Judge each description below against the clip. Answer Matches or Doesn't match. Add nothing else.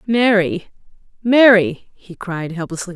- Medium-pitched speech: Doesn't match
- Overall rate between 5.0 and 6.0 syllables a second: Doesn't match